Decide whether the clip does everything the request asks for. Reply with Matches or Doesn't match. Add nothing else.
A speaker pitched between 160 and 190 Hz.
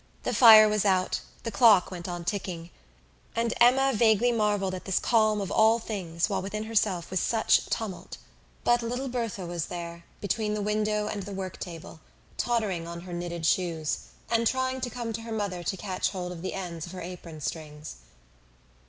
Doesn't match